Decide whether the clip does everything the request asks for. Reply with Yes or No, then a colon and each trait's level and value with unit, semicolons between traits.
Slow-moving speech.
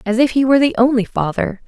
No: fast, 250 wpm